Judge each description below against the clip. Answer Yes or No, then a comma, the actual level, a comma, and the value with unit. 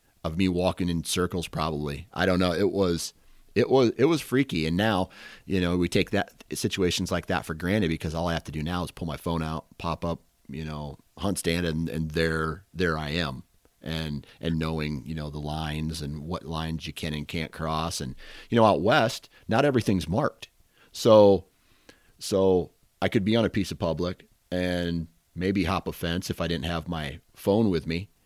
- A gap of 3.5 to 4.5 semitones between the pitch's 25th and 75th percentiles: No, average, 2.7 semitones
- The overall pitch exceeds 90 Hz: No, very low, 85 Hz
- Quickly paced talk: Yes, fast, 210 wpm